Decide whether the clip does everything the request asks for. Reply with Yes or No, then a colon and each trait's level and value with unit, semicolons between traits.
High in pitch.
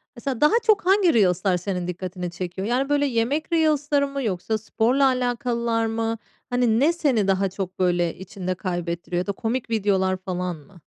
Yes: high, 220 Hz